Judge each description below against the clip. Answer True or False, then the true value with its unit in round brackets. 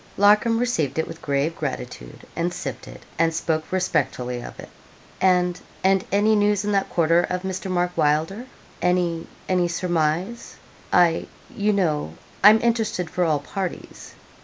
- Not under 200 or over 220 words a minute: False (150 wpm)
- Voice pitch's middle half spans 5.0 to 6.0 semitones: False (3.7 semitones)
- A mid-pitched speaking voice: True (180 Hz)